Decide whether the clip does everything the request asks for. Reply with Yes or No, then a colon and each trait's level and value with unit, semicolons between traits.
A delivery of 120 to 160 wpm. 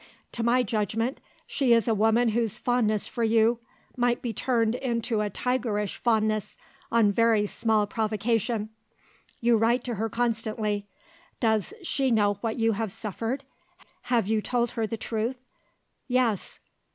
Yes: average, 145 wpm